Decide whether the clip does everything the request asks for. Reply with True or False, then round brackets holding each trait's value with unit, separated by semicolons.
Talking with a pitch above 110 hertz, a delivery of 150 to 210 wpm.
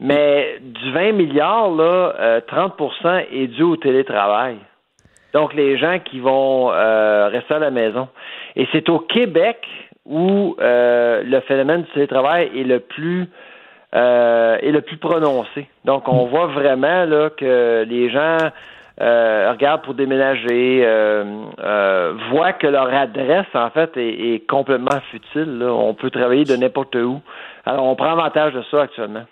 True (135 Hz; 160 wpm)